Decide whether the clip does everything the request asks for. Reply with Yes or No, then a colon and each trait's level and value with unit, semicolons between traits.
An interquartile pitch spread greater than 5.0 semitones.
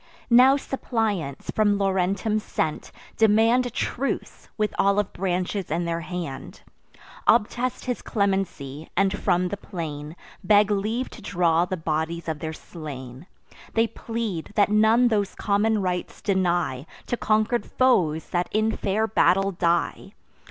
No: average, 4.4 semitones